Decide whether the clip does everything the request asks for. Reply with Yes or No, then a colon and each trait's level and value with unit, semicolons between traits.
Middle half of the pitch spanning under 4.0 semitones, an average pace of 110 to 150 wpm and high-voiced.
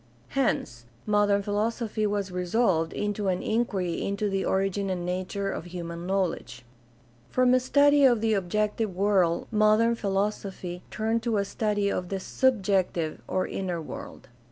Yes: average, 3.0 semitones; average, 145 wpm; high, 200 Hz